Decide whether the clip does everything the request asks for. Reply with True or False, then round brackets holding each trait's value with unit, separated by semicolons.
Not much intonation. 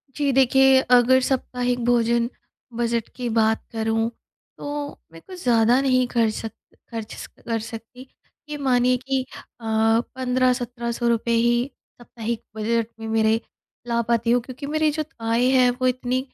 True (2.0 semitones)